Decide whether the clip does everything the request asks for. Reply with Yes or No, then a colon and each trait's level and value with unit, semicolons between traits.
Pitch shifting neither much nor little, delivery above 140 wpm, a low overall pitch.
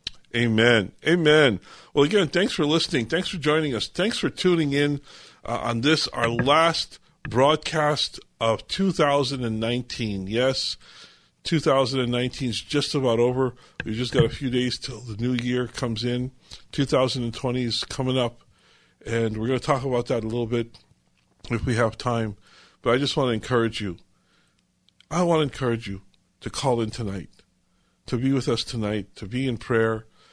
Yes: average, 3.9 semitones; average, 165 wpm; low, 125 Hz